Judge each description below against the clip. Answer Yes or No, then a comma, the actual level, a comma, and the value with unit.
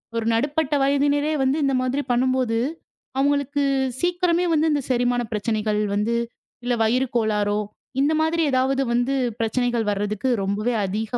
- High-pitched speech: Yes, very high, 250 Hz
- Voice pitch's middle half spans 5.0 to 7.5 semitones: No, average, 4.3 semitones